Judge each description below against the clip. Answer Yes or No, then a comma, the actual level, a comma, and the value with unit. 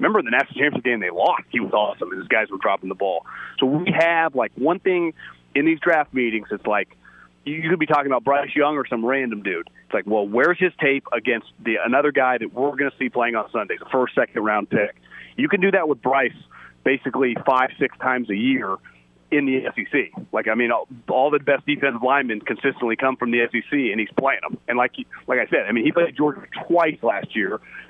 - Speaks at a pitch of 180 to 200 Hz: No, low, 135 Hz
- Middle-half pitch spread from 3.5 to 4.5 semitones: Yes, average, 3.9 semitones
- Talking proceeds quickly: Yes, fast, 235 wpm